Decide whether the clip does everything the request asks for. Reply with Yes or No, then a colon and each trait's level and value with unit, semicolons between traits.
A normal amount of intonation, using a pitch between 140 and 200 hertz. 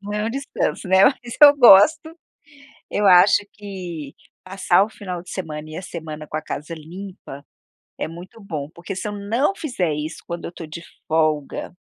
Yes: average, 4.6 semitones; medium, 185 Hz